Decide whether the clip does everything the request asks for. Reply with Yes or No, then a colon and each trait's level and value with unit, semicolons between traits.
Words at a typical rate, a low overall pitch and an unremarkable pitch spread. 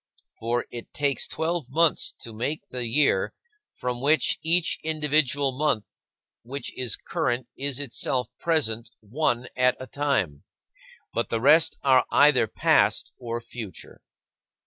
No: slow, 130 wpm; low, 130 Hz; average, 4.0 semitones